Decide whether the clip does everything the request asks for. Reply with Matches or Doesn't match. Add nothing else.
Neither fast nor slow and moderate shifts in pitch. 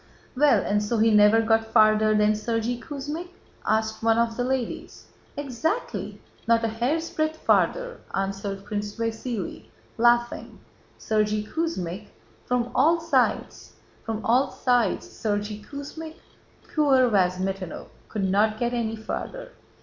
Doesn't match